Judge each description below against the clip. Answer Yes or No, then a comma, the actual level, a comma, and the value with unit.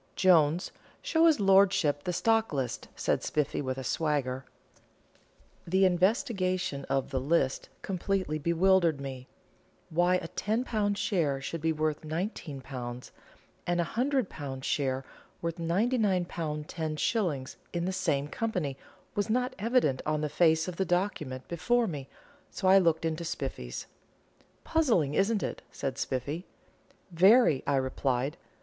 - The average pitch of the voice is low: No, medium, 165 Hz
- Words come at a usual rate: No, slow, 130 wpm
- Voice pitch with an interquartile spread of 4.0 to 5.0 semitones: No, wide, 5.4 semitones